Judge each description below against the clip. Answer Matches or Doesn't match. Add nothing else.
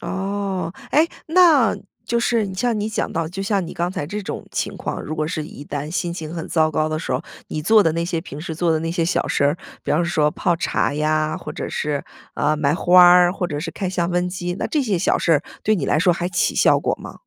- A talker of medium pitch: Matches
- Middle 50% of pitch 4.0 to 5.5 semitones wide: Doesn't match